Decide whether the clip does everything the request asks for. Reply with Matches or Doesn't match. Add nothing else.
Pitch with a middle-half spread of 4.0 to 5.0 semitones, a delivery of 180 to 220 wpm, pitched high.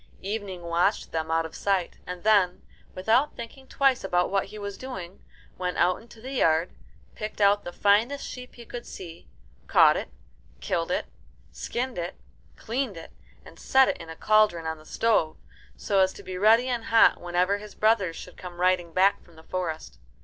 Matches